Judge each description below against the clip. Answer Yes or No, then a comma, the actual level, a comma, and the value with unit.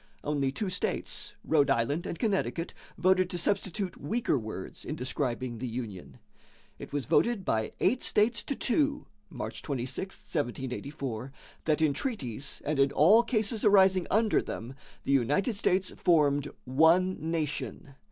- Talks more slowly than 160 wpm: Yes, average, 140 wpm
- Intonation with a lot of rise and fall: Yes, wide, 6.4 semitones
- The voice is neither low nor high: Yes, medium, 155 Hz